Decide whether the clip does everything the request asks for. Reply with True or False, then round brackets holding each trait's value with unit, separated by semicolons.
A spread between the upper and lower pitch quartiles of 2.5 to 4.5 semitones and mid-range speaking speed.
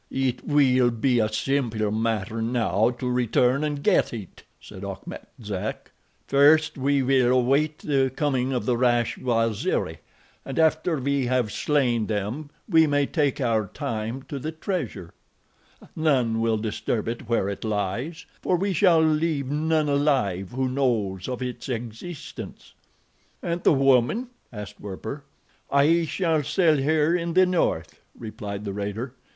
False (4.9 semitones; 145 wpm)